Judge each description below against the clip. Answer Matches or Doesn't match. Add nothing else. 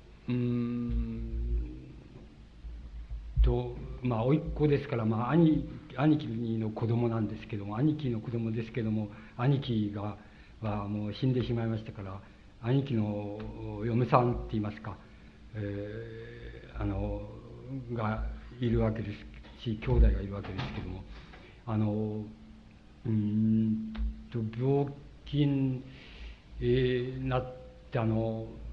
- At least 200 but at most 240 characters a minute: Matches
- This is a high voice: Doesn't match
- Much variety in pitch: Doesn't match